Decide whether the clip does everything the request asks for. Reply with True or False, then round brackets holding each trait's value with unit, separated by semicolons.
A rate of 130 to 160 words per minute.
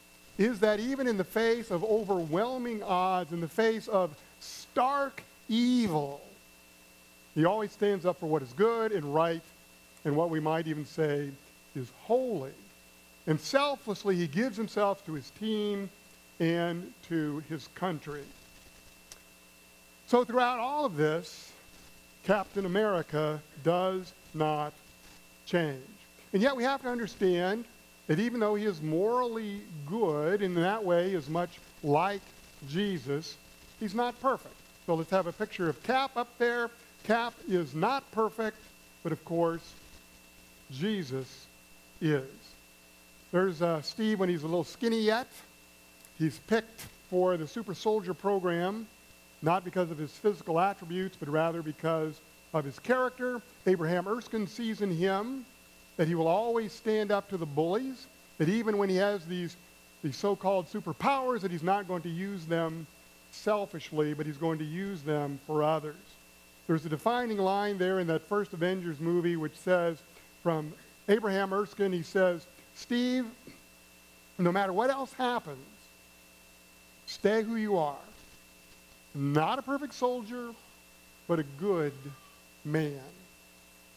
True (140 wpm)